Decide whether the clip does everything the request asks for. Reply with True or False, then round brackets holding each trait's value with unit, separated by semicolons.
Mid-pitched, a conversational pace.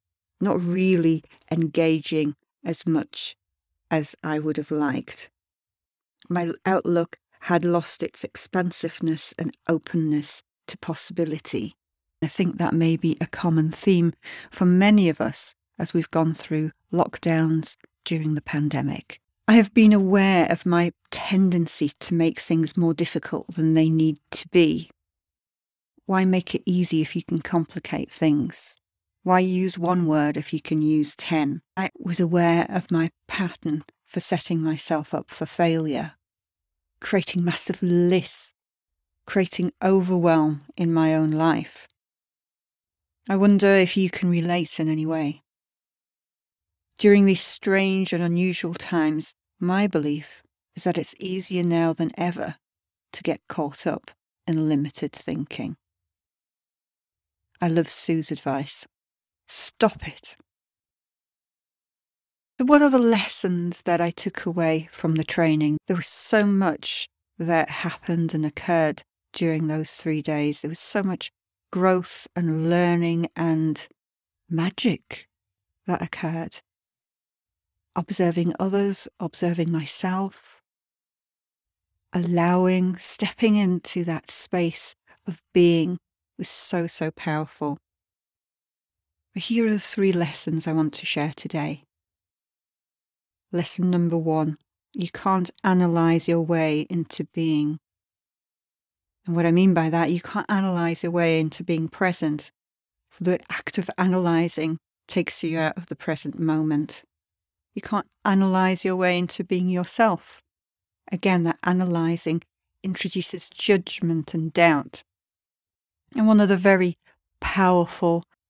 False (165 Hz; 125 wpm)